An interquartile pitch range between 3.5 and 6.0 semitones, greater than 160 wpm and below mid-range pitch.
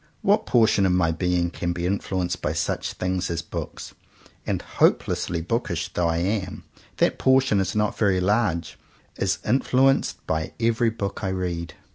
Yes: average, 4.1 semitones; average, 170 wpm; very low, 95 Hz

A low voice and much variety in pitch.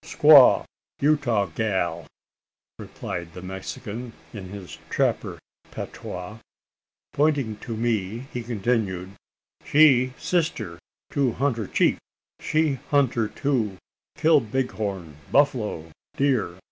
Yes: low, 115 Hz; wide, 6.3 semitones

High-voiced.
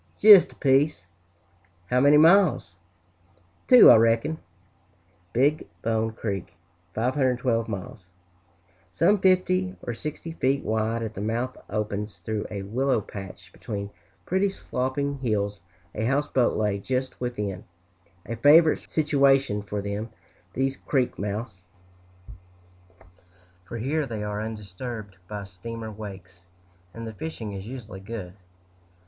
No: low, 115 Hz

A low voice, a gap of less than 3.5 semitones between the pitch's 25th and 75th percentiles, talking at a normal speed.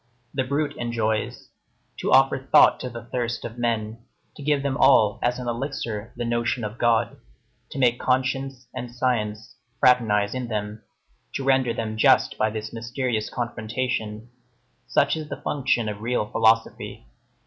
Yes: low, 120 Hz; average, 2.8 semitones; average, 155 wpm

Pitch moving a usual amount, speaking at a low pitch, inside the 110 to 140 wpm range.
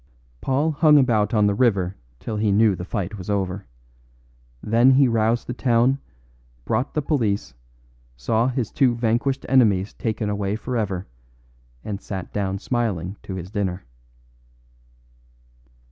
Yes: average, 3.9 semitones; low, 110 Hz; slow, 135 wpm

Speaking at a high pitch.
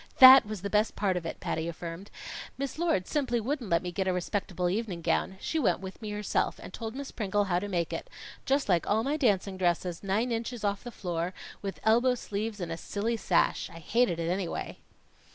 Yes: high, 200 Hz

